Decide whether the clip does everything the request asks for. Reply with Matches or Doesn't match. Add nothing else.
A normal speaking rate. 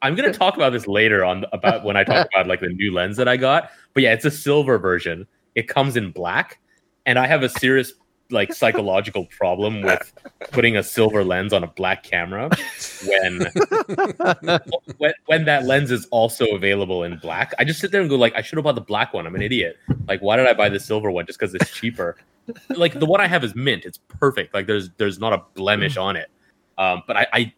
Doesn't match